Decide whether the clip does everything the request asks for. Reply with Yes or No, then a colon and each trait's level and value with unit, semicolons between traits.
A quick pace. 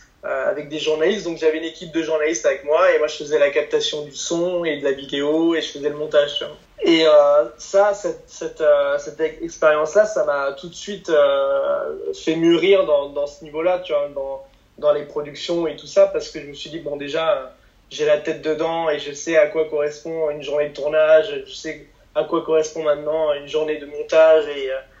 Yes: fast, 230 wpm